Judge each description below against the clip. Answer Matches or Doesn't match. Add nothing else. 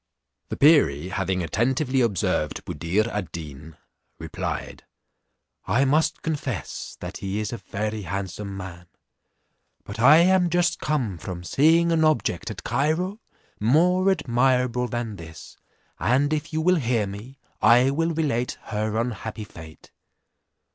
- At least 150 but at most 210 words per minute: Doesn't match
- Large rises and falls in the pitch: Matches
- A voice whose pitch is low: Matches